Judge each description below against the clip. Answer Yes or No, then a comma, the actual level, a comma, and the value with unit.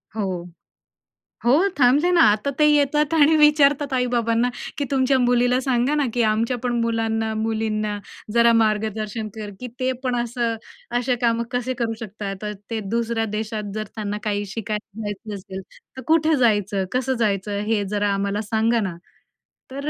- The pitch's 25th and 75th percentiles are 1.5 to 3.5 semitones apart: Yes, average, 3.2 semitones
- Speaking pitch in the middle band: No, high, 230 Hz